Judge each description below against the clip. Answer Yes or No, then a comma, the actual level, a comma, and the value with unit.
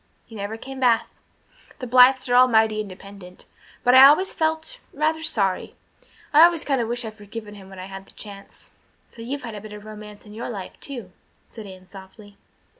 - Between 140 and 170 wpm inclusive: No, average, 200 wpm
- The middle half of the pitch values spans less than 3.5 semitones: No, average, 4.3 semitones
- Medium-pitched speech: No, high, 220 Hz